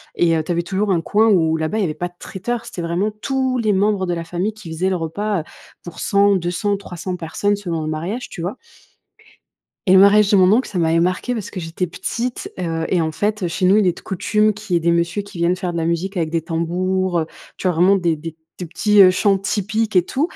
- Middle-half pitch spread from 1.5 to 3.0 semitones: No, average, 3.4 semitones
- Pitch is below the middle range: No, medium, 185 Hz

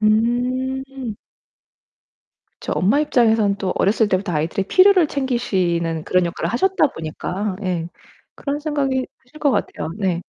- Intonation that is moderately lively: No, wide, 6.3 semitones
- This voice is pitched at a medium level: No, high, 220 Hz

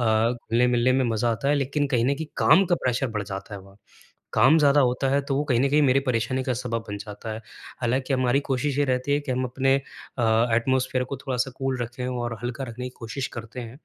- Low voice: Yes, low, 125 Hz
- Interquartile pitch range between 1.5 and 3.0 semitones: Yes, narrow, 2.6 semitones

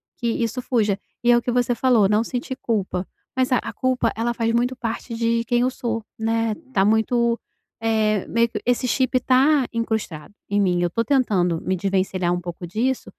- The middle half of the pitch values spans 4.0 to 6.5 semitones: No, average, 3.2 semitones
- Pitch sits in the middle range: No, high, 230 Hz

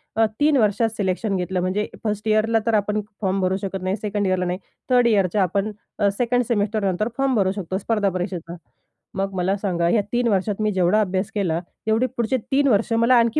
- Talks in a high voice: Yes, high, 205 Hz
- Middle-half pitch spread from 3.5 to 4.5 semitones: No, average, 3.0 semitones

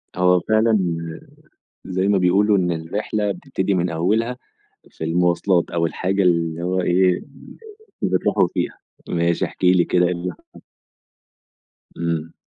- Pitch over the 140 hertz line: No, very low, 90 Hz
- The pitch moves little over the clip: Yes, narrow, 2.2 semitones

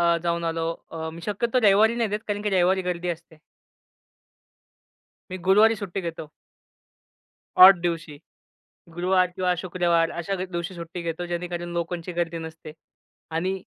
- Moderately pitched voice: Yes, medium, 175 Hz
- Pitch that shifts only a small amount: Yes, narrow, 2.2 semitones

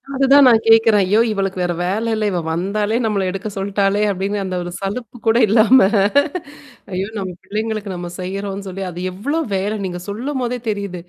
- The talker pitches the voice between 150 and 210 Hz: Yes, high, 200 Hz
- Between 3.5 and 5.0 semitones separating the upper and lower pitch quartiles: No, average, 2.9 semitones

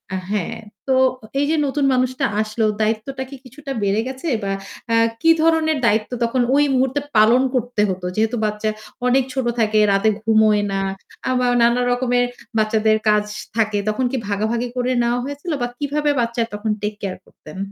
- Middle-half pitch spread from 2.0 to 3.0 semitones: No, average, 3.5 semitones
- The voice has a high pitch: Yes, high, 235 Hz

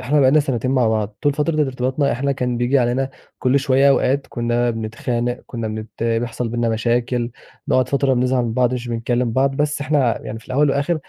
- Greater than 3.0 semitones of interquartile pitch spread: No, average, 2.7 semitones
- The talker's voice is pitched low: Yes, low, 125 Hz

